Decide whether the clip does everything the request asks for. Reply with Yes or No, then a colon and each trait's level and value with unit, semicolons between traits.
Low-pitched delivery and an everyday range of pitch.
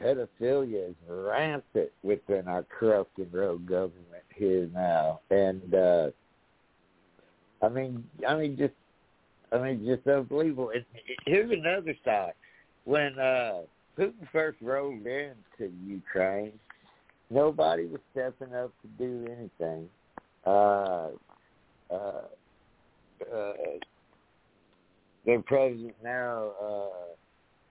No: low, 120 Hz; wide, 6.2 semitones